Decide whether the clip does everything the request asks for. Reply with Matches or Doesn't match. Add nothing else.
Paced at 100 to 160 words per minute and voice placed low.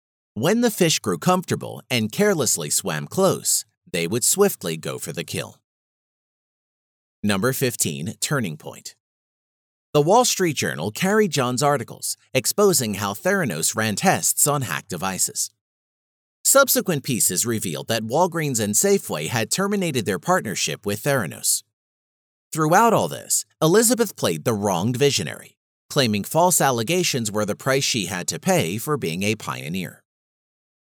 Matches